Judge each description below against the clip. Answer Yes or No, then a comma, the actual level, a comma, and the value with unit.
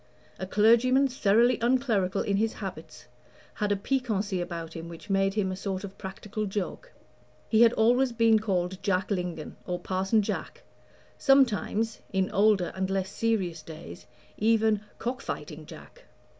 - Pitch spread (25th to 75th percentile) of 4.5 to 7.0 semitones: No, average, 3.3 semitones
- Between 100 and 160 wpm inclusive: Yes, average, 150 wpm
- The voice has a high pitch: Yes, high, 200 Hz